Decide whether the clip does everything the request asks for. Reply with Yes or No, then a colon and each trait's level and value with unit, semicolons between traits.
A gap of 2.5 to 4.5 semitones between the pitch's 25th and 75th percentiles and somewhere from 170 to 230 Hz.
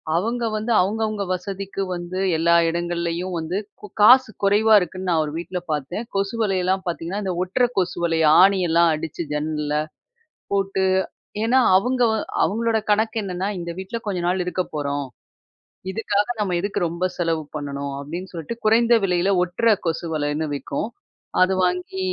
Yes: average, 3.4 semitones; medium, 185 Hz